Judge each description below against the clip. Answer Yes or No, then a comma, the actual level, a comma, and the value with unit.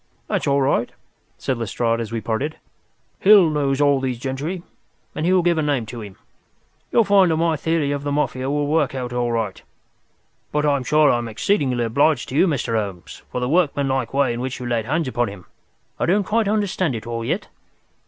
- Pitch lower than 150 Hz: Yes, medium, 140 Hz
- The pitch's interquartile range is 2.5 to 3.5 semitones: No, average, 4.7 semitones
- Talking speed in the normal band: No, fast, 210 wpm